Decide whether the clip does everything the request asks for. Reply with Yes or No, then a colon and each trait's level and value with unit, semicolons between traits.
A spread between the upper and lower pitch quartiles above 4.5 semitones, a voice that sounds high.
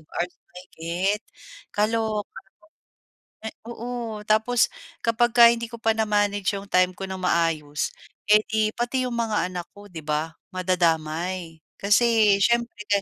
No: average, 4.0 semitones; high, 205 Hz